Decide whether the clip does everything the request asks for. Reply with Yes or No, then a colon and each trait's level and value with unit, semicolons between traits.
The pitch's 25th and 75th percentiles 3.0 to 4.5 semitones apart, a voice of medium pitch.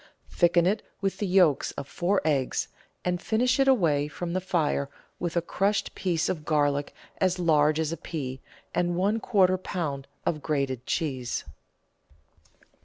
Yes: average, 4.1 semitones; medium, 170 Hz